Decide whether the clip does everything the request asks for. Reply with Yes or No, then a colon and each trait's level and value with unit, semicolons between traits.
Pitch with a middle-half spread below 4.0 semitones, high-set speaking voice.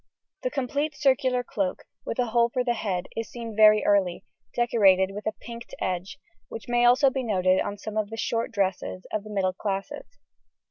Yes: average, 3.6 semitones; high, 220 Hz